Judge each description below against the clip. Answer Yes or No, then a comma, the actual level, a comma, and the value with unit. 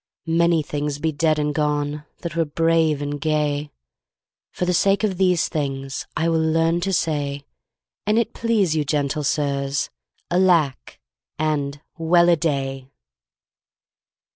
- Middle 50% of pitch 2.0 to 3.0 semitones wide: Yes, narrow, 2.6 semitones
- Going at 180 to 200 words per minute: No, average, 140 wpm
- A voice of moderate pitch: Yes, medium, 155 Hz